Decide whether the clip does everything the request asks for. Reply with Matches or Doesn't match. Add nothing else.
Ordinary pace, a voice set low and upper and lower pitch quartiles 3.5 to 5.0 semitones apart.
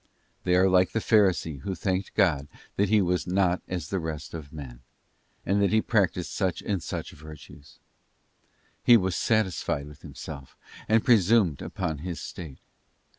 Matches